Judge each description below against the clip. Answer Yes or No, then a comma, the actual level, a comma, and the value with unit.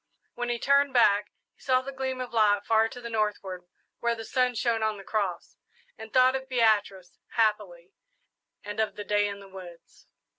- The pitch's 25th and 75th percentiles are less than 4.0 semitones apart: Yes, average, 3.3 semitones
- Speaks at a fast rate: No, average, 190 wpm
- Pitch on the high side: Yes, high, 220 Hz